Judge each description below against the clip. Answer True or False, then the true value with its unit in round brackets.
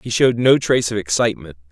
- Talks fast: True (210 wpm)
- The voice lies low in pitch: True (105 Hz)